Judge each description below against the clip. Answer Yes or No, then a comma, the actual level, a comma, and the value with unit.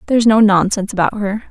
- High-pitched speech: Yes, high, 205 Hz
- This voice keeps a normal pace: No, fast, 240 wpm